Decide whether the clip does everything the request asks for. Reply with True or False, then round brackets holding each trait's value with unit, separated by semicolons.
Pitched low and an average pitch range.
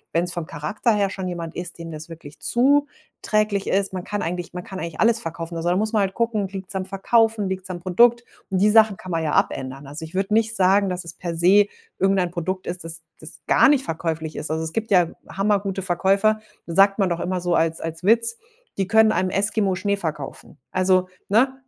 False (190 Hz; 3.6 semitones)